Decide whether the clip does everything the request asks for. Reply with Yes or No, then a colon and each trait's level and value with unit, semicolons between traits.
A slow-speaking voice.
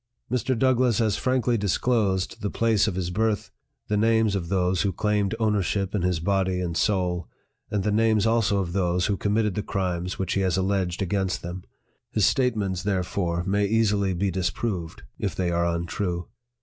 No: average, 180 wpm